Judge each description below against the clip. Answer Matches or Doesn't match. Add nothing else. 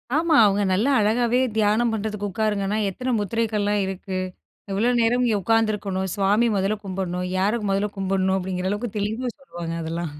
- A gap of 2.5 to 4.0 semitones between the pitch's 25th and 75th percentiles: Matches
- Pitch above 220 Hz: Doesn't match